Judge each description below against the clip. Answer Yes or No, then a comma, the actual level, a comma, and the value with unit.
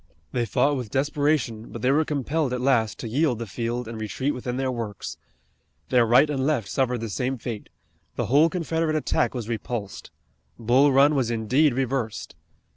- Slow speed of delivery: No, average, 180 wpm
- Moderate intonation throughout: Yes, average, 3.5 semitones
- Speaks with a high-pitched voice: No, low, 125 Hz